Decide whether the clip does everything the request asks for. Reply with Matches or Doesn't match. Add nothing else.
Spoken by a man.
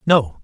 Matches